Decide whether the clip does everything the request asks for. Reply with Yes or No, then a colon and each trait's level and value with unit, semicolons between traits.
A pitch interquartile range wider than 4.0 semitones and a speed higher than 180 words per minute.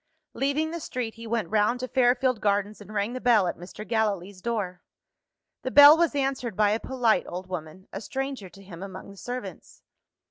Yes: average, 4.4 semitones; average, 190 wpm